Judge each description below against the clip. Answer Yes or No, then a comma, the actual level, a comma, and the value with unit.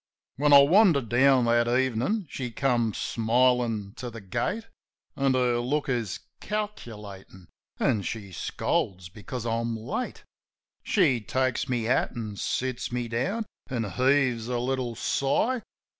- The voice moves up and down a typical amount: Yes, average, 3.1 semitones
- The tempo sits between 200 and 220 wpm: No, slow, 135 wpm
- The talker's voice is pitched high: No, low, 125 Hz